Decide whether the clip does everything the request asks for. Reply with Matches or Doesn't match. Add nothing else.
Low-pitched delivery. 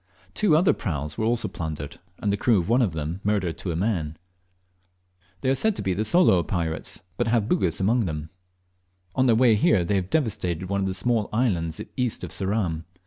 Matches